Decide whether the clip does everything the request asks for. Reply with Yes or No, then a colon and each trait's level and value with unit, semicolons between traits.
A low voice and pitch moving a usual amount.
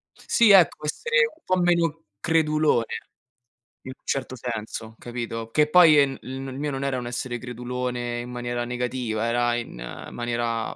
Yes: low, 125 Hz; average, 4.0 semitones